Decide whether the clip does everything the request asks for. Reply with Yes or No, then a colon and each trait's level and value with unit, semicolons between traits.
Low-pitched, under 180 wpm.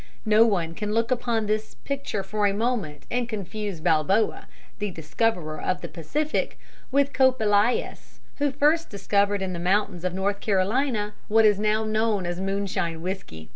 No: high, 210 Hz; average, 165 wpm